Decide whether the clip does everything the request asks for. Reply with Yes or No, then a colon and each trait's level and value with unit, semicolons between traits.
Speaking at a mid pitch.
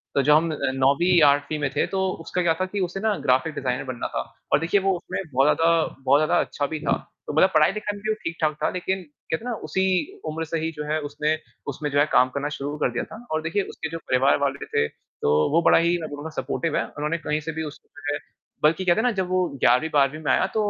Yes: medium, 155 Hz